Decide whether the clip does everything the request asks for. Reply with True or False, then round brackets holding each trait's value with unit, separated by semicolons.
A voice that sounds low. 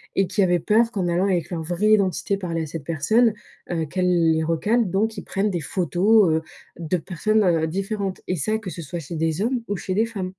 False (185 Hz)